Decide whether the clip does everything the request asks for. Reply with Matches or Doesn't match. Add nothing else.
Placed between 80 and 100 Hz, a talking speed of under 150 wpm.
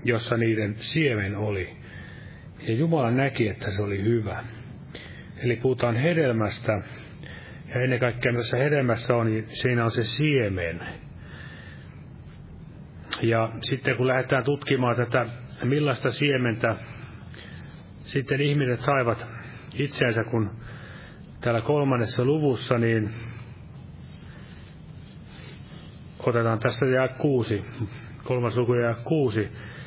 Doesn't match